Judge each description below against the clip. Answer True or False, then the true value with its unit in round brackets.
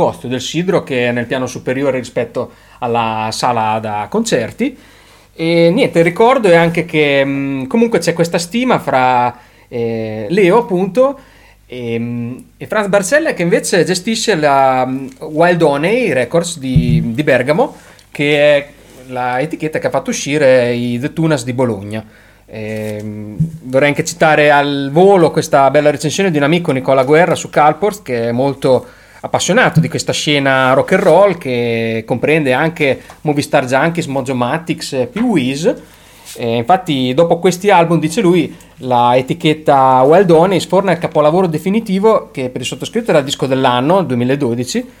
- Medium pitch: True (145 Hz)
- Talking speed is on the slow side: False (150 wpm)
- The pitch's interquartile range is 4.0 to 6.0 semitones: True (5.2 semitones)